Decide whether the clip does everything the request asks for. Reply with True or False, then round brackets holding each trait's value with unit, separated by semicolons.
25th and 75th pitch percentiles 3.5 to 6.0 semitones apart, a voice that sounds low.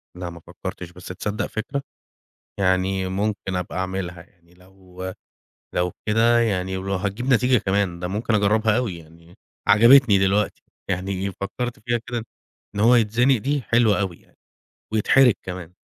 True (3.8 semitones; 100 Hz)